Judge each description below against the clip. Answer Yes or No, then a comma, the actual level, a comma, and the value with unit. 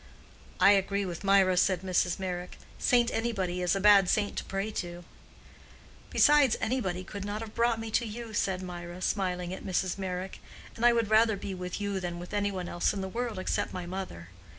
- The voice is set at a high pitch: Yes, high, 195 Hz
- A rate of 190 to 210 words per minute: Yes, average, 200 wpm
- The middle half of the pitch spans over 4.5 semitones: No, average, 2.9 semitones